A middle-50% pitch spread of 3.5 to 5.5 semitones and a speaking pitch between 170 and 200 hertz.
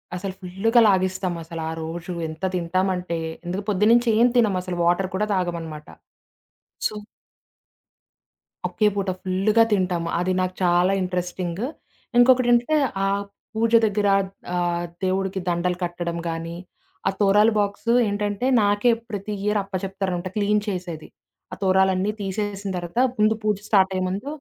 No: average, 2.7 semitones; high, 190 Hz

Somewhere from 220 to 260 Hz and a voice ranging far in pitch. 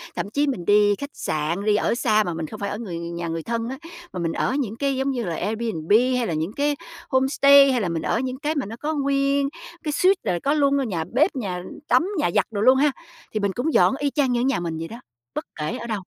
Yes: high, 235 Hz; wide, 7.1 semitones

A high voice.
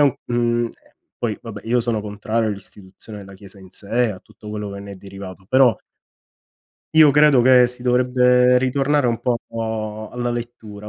No: low, 115 Hz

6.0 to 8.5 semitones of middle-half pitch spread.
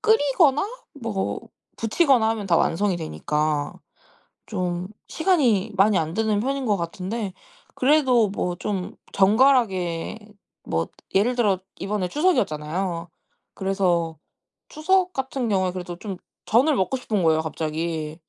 Yes: wide, 6.3 semitones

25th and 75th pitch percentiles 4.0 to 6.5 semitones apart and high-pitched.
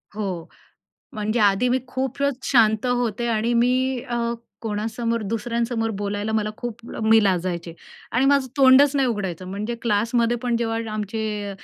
No: average, 2.8 semitones; high, 230 Hz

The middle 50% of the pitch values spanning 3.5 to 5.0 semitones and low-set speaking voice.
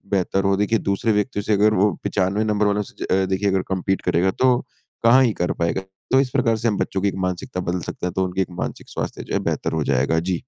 No: average, 2.7 semitones; low, 100 Hz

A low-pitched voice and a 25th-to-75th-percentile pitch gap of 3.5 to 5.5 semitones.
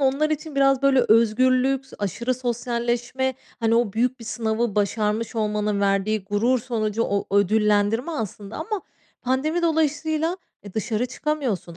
No: high, 235 Hz; average, 4.1 semitones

